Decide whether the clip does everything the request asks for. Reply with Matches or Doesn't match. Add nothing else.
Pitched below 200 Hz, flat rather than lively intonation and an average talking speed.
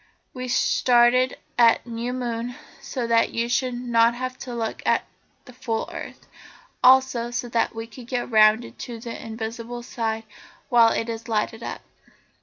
Doesn't match